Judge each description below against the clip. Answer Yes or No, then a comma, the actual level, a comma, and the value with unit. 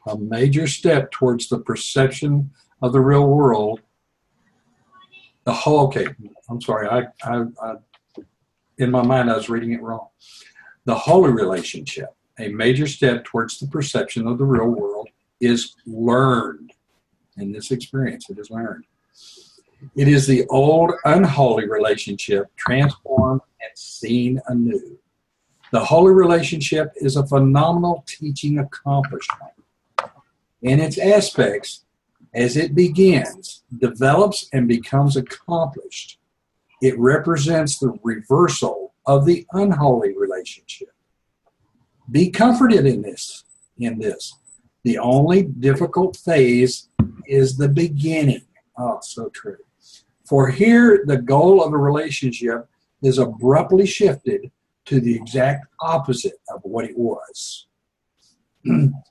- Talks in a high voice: No, low, 135 Hz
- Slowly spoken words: Yes, slow, 120 wpm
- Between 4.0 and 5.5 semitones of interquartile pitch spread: Yes, average, 4.6 semitones